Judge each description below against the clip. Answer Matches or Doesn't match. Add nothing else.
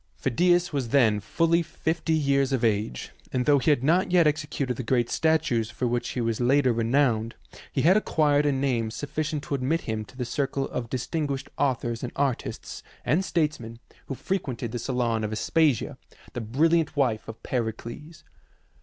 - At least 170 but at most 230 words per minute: Matches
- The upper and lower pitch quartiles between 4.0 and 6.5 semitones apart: Matches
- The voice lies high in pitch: Doesn't match